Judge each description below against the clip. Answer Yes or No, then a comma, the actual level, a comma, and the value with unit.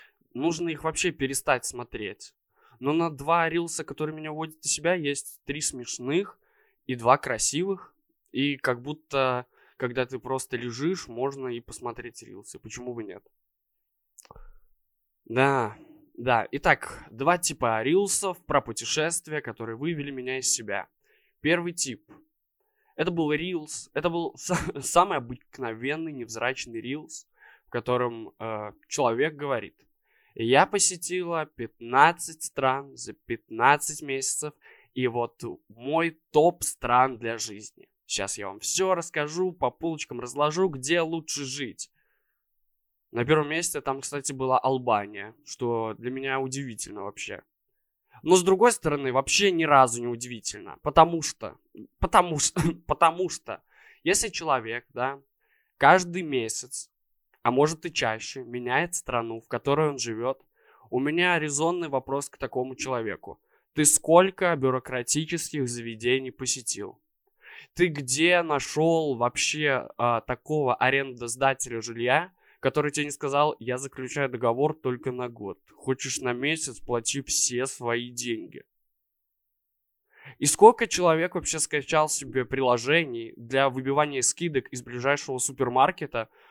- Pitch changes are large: No, average, 4.5 semitones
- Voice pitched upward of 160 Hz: No, medium, 140 Hz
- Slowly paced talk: No, average, 125 wpm